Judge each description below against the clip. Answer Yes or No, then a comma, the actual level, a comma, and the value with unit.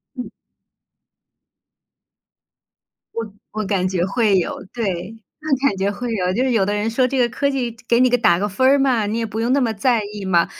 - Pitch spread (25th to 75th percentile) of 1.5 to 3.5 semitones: No, average, 3.9 semitones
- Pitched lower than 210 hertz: No, high, 225 Hz